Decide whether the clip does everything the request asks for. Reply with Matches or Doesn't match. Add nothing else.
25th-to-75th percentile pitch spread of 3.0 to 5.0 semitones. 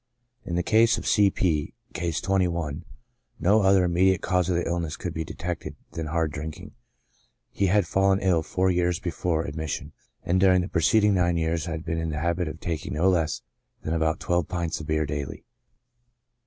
Doesn't match